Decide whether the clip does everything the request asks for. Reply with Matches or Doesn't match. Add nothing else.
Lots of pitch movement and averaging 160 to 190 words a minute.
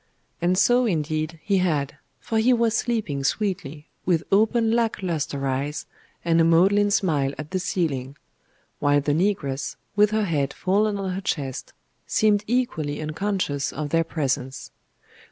Doesn't match